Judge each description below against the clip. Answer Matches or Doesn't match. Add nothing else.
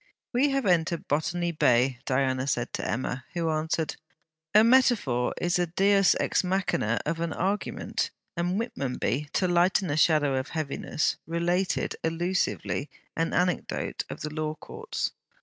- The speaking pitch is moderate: Matches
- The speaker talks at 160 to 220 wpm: Doesn't match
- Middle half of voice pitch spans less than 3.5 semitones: Doesn't match